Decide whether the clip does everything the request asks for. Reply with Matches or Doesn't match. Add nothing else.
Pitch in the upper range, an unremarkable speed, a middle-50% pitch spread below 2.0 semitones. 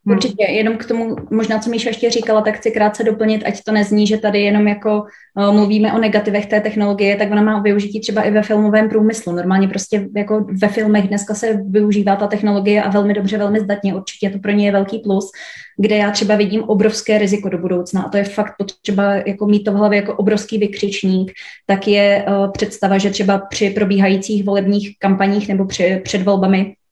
Doesn't match